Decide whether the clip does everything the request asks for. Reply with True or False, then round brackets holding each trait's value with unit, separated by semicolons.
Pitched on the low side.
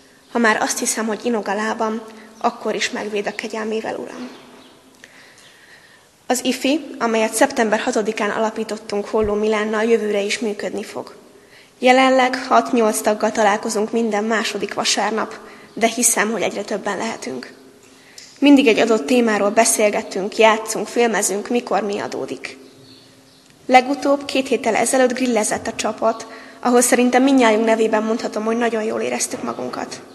False (220 Hz)